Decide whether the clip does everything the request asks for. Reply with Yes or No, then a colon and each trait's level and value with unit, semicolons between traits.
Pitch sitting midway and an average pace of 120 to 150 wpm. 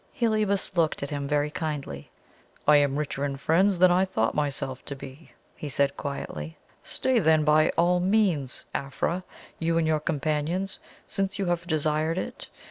No: medium, 155 Hz; average, 165 wpm